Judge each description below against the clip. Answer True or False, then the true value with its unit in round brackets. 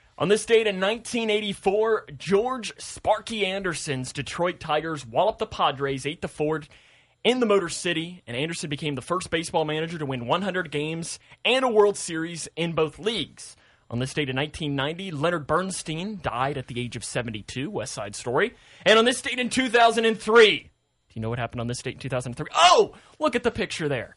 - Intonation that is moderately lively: False (7.0 semitones)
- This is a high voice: False (165 Hz)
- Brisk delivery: False (190 wpm)